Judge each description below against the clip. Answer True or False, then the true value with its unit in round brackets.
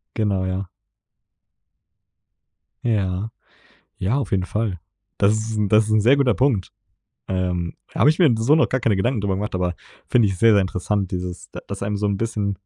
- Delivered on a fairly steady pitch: False (3.1 semitones)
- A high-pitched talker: False (105 Hz)